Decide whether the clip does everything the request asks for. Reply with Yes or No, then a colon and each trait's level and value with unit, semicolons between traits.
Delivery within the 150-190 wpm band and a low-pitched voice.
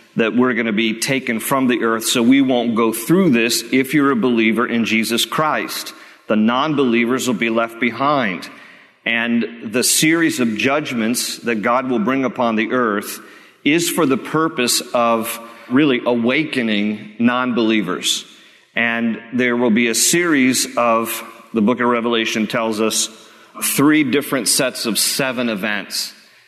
Yes: average, 155 wpm; low, 120 Hz